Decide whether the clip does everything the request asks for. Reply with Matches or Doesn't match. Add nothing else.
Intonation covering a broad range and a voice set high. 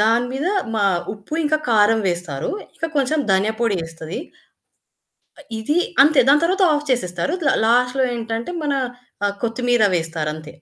Matches